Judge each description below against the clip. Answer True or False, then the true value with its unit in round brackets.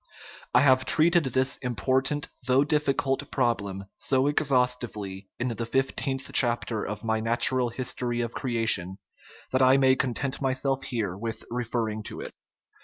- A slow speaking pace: False (155 wpm)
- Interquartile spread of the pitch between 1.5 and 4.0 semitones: True (2.8 semitones)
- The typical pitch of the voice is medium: False (125 Hz)